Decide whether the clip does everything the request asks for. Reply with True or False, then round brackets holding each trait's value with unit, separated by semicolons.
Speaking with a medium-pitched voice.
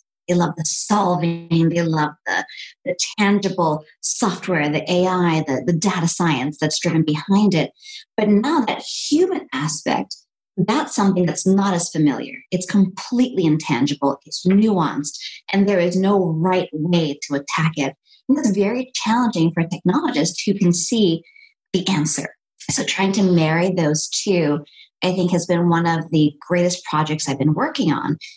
True (180 Hz)